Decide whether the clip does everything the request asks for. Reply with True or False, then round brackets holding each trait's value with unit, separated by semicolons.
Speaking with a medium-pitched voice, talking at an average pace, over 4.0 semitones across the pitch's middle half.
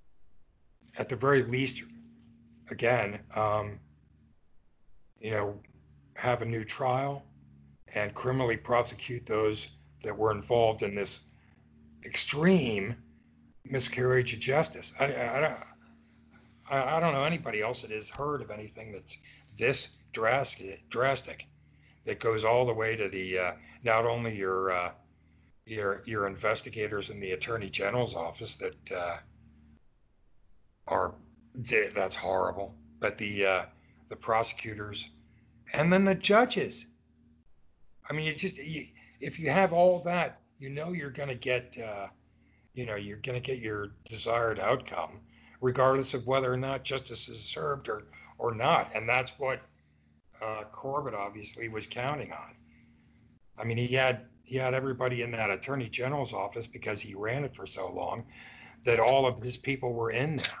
False (115 Hz; 145 wpm; 5.0 semitones)